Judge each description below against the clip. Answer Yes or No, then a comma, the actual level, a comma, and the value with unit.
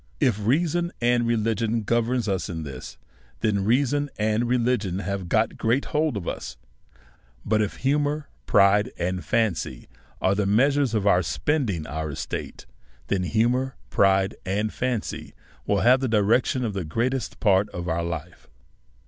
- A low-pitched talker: Yes, low, 110 Hz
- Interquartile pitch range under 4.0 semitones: No, average, 4.7 semitones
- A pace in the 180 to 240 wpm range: No, average, 150 wpm